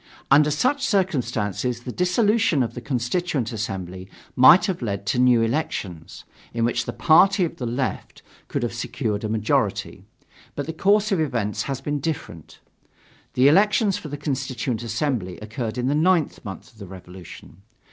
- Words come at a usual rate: Yes, average, 165 wpm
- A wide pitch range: Yes, wide, 6.5 semitones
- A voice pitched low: Yes, low, 125 Hz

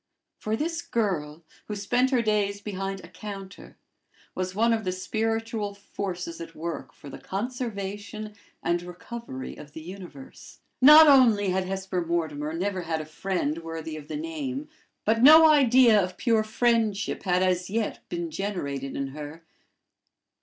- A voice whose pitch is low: No, high, 195 Hz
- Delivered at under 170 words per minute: Yes, average, 155 wpm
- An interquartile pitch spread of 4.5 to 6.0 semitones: Yes, average, 4.9 semitones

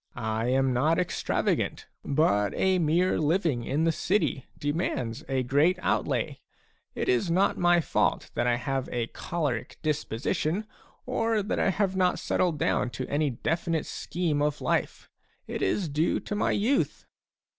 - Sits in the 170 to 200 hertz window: No, medium, 155 Hz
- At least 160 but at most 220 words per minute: No, average, 150 wpm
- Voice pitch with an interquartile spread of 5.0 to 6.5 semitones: Yes, average, 5.3 semitones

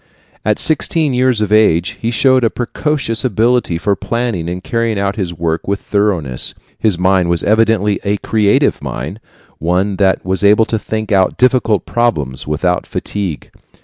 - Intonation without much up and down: No, average, 4.1 semitones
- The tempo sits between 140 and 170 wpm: Yes, average, 160 wpm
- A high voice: No, low, 105 Hz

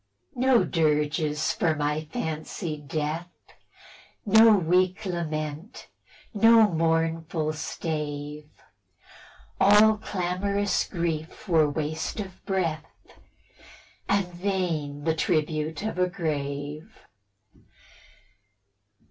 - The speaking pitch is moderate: Yes, medium, 165 Hz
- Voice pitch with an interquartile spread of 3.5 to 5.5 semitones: Yes, average, 3.9 semitones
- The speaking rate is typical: No, slow, 80 wpm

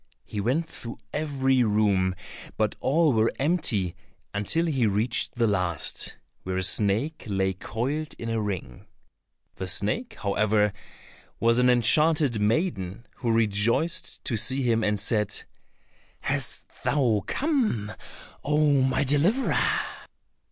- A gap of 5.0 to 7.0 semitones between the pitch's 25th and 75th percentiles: Yes, wide, 5.6 semitones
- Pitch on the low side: Yes, low, 115 Hz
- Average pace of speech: No, slow, 125 wpm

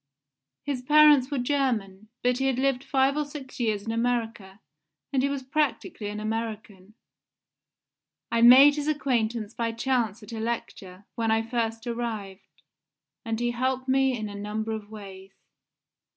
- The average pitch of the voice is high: Yes, high, 235 Hz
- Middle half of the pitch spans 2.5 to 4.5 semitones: Yes, average, 3.4 semitones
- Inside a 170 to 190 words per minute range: No, average, 155 wpm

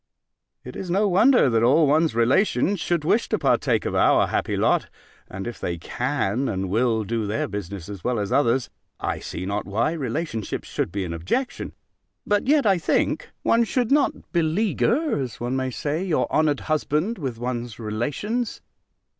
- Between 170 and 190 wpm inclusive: Yes, average, 175 wpm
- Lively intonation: Yes, wide, 8.6 semitones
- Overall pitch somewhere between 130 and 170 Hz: Yes, low, 135 Hz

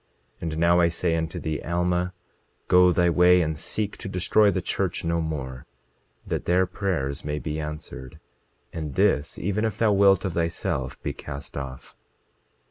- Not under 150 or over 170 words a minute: Yes, average, 165 wpm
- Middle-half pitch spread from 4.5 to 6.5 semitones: No, average, 3.2 semitones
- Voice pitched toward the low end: Yes, very low, 85 Hz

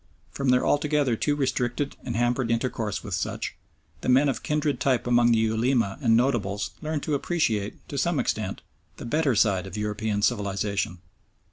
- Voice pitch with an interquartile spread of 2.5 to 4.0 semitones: No, average, 4.7 semitones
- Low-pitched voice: Yes, low, 120 Hz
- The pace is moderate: Yes, average, 165 wpm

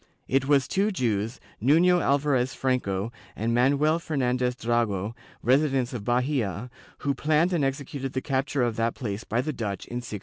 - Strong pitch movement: No, average, 3.3 semitones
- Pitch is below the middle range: Yes, low, 130 Hz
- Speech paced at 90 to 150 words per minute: No, average, 165 wpm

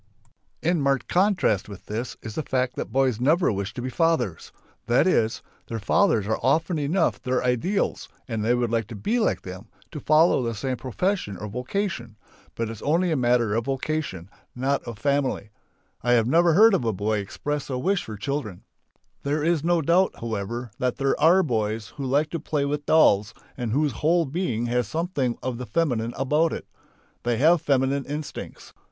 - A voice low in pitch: Yes, low, 130 Hz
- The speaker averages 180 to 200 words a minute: Yes, average, 190 wpm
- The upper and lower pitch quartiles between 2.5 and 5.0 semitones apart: No, wide, 5.5 semitones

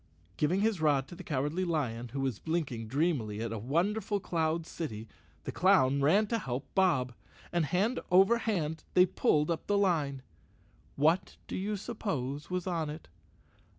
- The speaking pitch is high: No, medium, 160 Hz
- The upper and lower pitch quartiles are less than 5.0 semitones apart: No, wide, 5.4 semitones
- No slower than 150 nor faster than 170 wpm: Yes, average, 165 wpm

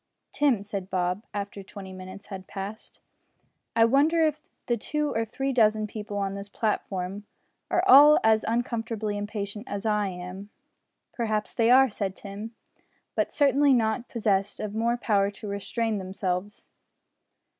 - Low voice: No, high, 210 Hz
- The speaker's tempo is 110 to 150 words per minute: Yes, average, 145 wpm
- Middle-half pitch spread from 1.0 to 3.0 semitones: Yes, average, 2.7 semitones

